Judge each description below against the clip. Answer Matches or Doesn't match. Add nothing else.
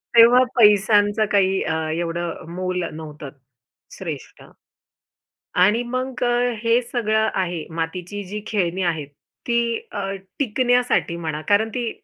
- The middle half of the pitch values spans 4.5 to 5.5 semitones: Matches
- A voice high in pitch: Matches